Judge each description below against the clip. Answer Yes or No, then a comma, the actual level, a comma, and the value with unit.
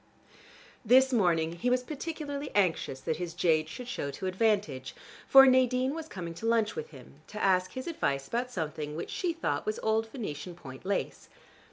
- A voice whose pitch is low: No, high, 205 Hz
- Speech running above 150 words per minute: Yes, average, 180 wpm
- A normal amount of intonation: No, wide, 7.9 semitones